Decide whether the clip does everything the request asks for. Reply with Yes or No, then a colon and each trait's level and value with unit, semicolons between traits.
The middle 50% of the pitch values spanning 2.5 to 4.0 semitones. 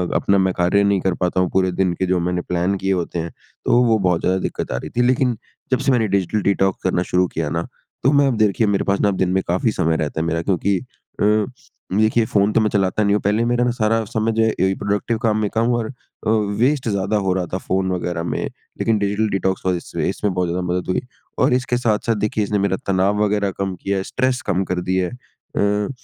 Yes: average, 2.9 semitones